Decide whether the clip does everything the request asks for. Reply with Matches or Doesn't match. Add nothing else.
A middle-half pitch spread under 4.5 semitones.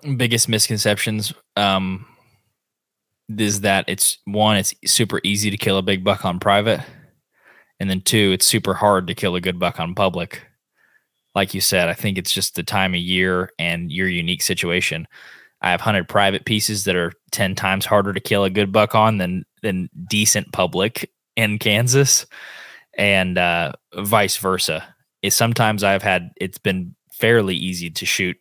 Matches